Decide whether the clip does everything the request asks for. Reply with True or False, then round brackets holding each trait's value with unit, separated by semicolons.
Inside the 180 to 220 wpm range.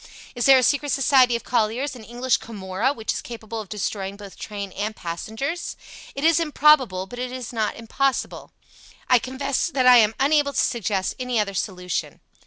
True (185 wpm)